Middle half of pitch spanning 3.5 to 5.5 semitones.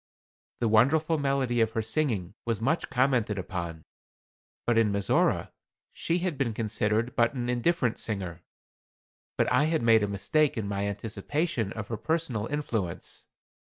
Yes: average, 5.1 semitones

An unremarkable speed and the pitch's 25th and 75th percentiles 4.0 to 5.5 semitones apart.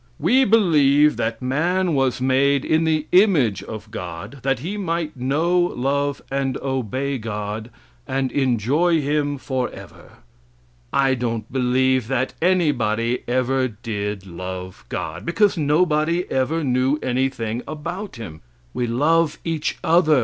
No: slow, 130 wpm; average, 4.7 semitones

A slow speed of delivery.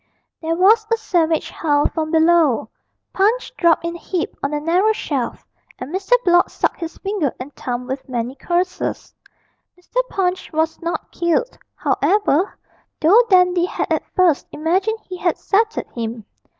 No: average, 155 wpm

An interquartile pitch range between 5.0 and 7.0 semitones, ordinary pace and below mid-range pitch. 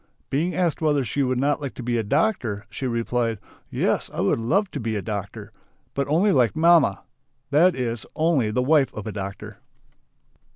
Yes: wide, 5.6 semitones; average, 190 wpm; low, 130 Hz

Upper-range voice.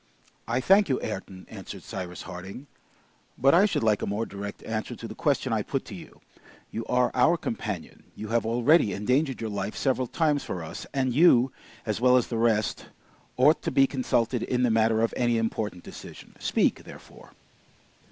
No: low, 115 Hz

